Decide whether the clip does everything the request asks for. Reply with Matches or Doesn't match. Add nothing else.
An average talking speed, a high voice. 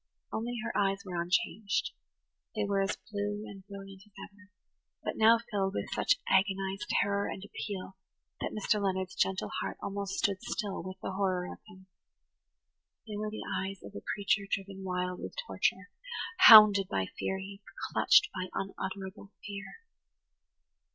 Matches